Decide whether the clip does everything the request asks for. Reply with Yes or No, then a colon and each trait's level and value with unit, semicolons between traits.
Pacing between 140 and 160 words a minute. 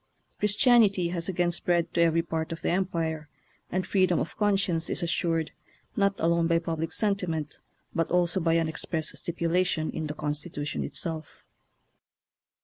Yes: average, 150 wpm